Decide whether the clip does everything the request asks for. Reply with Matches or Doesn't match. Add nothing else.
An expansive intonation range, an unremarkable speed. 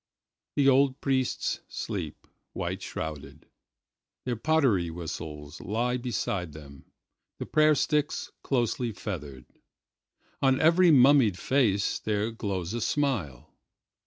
Doesn't match